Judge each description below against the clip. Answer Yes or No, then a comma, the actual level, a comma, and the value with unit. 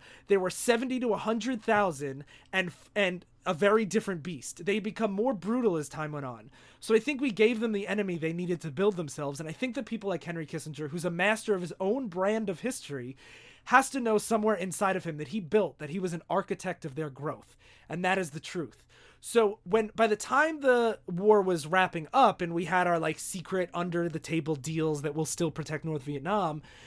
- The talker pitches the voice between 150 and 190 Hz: Yes, medium, 185 Hz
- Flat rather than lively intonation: No, average, 5.1 semitones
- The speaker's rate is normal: No, fast, 225 wpm